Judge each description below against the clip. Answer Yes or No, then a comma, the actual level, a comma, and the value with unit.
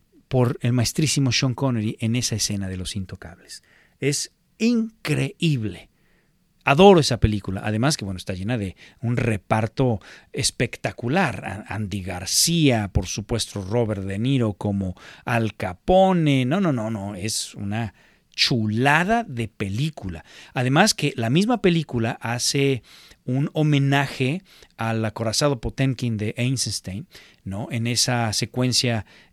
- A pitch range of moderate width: Yes, average, 4.9 semitones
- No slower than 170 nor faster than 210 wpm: No, slow, 125 wpm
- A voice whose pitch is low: Yes, low, 115 Hz